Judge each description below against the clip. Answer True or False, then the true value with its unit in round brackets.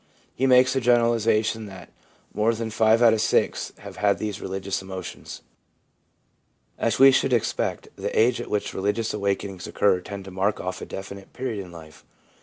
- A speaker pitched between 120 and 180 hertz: False (105 Hz)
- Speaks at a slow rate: False (180 wpm)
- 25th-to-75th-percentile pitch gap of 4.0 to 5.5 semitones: False (3.1 semitones)